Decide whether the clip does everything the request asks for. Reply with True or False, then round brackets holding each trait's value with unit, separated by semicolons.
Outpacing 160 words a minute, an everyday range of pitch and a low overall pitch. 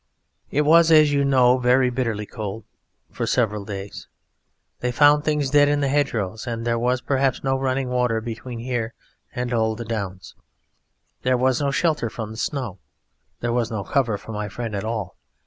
True (180 wpm; 3.4 semitones; 125 Hz)